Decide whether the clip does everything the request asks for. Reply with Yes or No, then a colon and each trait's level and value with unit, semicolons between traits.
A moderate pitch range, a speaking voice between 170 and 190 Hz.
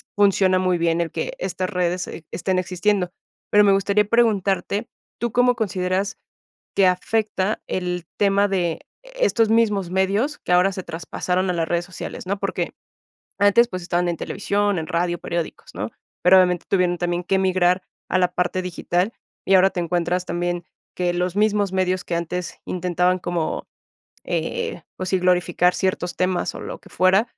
No: narrow, 2.1 semitones; medium, 185 Hz